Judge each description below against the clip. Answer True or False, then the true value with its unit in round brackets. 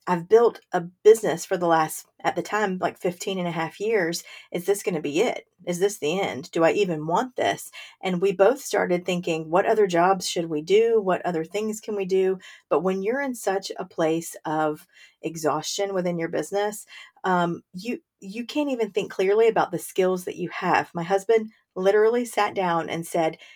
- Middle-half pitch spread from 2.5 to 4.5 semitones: True (3.7 semitones)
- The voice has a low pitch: False (190 Hz)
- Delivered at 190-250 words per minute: True (205 wpm)